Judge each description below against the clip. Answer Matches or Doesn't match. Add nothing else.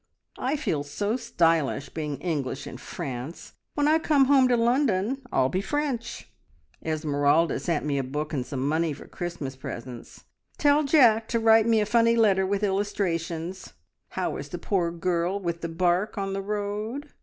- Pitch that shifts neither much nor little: Doesn't match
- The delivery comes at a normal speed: Matches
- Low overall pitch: Doesn't match